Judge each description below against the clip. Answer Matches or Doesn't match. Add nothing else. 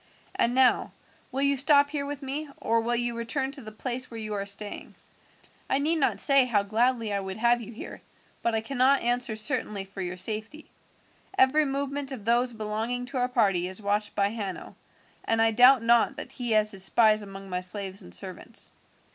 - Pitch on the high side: Matches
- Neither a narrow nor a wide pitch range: Matches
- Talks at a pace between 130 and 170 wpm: Doesn't match